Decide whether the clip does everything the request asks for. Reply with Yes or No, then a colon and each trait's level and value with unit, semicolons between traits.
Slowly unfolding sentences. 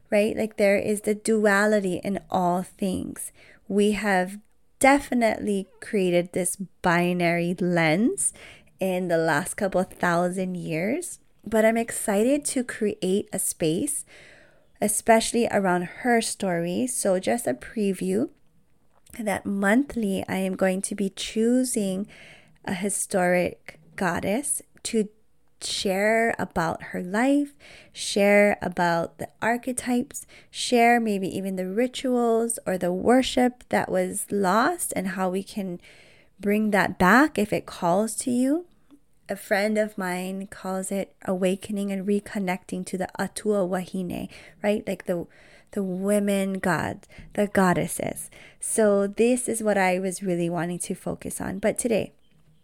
Yes: slow, 130 wpm